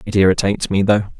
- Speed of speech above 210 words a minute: No, average, 200 wpm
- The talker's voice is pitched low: Yes, low, 100 Hz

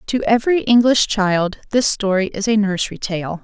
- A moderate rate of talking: Yes, average, 175 wpm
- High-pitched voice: Yes, high, 210 Hz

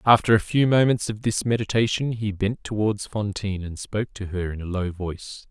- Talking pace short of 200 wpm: No, fast, 205 wpm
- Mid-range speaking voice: No, low, 105 Hz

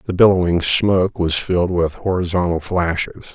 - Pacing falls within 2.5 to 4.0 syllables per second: No, 5.2 syllables/s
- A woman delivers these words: No, male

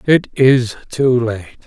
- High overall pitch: No, low, 125 Hz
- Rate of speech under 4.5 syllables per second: Yes, 3.6 syllables/s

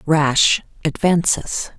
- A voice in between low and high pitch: Yes, medium, 160 Hz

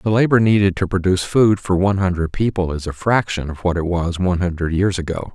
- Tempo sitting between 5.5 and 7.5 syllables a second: Yes, 6.0 syllables/s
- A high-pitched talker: No, very low, 95 Hz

